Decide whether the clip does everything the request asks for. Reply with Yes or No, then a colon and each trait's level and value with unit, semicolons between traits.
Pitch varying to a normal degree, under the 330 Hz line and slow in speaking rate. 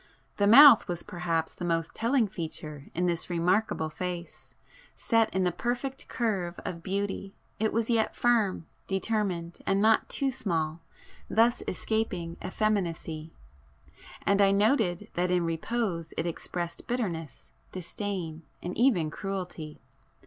Yes: average, 4.6 semitones; medium, 185 Hz; slow, 125 wpm